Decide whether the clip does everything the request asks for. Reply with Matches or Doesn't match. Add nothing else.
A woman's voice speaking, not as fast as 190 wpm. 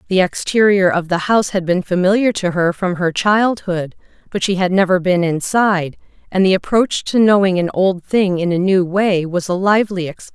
Doesn't match